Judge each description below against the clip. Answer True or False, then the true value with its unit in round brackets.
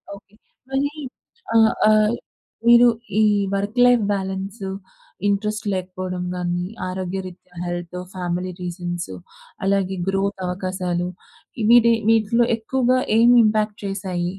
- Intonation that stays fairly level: False (3.2 semitones)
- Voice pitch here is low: False (195 Hz)